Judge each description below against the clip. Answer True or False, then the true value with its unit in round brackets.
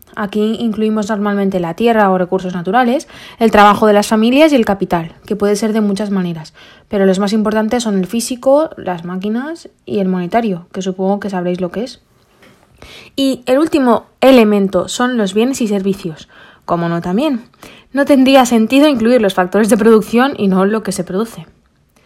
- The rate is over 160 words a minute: True (180 wpm)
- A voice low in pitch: False (210 Hz)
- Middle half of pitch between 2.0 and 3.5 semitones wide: False (4.1 semitones)